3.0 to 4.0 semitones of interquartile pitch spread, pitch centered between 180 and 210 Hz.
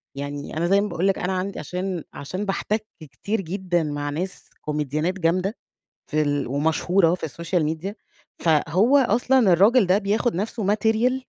No: average, 4.6 semitones; medium, 185 Hz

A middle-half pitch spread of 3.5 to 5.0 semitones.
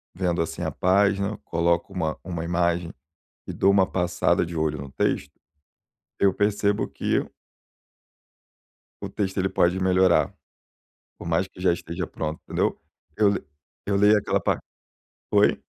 No: average, 2.7 semitones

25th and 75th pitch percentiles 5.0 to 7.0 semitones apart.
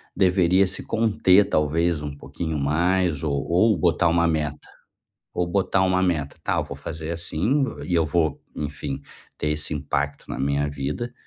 No: average, 3.7 semitones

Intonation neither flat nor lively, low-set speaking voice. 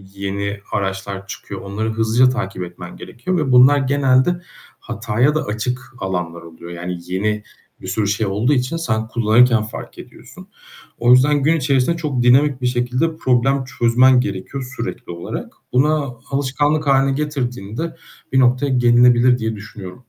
Yes: average, 4.3 semitones; low, 125 Hz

